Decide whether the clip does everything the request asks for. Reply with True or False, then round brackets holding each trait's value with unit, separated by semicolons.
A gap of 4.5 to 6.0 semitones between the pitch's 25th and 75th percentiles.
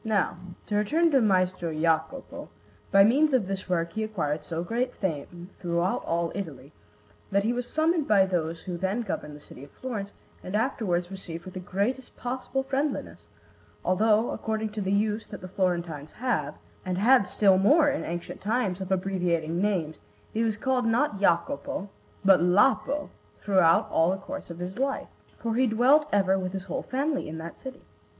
True (5.2 semitones)